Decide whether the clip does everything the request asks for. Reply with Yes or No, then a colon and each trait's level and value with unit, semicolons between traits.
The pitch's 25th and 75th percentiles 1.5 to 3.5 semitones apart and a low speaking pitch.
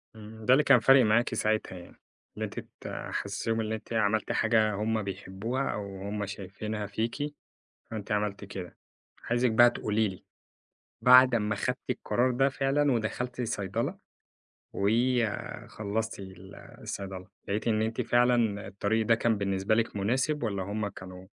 Yes: average, 3.0 semitones; low, 110 Hz